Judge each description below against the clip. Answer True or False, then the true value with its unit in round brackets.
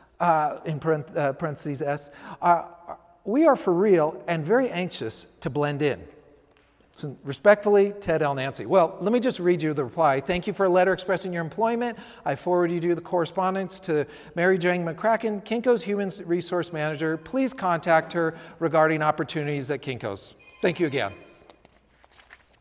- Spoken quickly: False (160 wpm)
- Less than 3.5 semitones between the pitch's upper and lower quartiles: False (3.8 semitones)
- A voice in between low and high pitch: True (170 Hz)